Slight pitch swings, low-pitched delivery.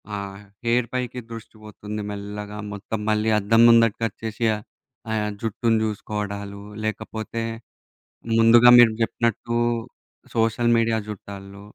Yes: narrow, 1.9 semitones; low, 110 Hz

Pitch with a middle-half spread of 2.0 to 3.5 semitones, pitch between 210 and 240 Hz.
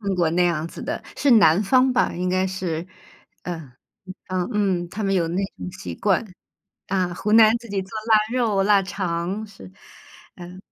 No: average, 3.0 semitones; high, 190 Hz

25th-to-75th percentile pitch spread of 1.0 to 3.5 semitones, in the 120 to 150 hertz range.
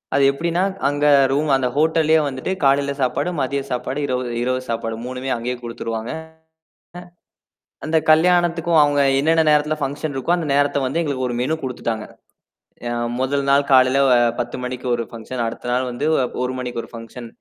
Yes: average, 3.2 semitones; low, 135 Hz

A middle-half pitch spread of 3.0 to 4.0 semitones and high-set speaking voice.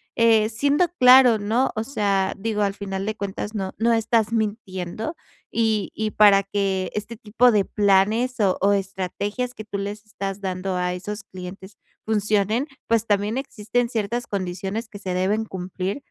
No: narrow, 2.6 semitones; high, 210 Hz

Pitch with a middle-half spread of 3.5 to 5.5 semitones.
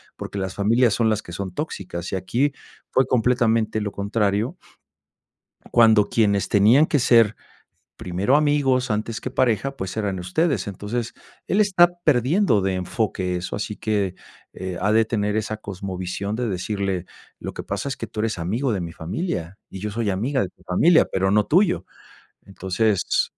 Yes: average, 4.2 semitones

